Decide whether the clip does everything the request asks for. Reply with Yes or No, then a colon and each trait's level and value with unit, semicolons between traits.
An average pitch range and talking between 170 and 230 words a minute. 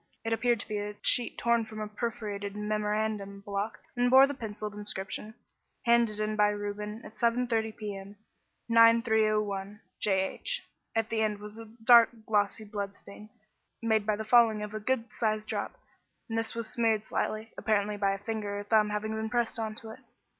No: narrow, 1.5 semitones; average, 180 wpm